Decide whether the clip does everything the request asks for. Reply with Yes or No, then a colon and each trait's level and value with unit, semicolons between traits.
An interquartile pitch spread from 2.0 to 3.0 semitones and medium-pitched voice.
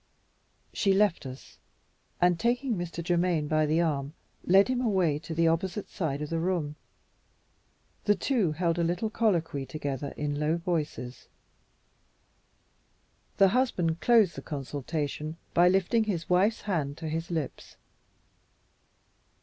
No: average, 4.1 semitones; medium, 170 Hz